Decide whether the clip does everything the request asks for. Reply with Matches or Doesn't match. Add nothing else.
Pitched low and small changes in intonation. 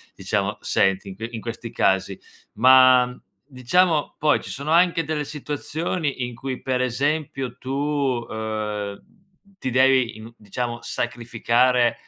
Doesn't match